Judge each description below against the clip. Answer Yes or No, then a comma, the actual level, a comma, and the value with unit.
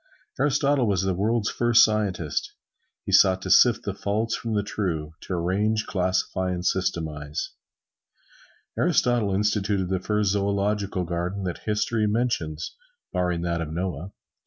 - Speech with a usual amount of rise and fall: Yes, average, 3.1 semitones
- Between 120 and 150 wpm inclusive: Yes, slow, 135 wpm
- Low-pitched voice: Yes, very low, 95 Hz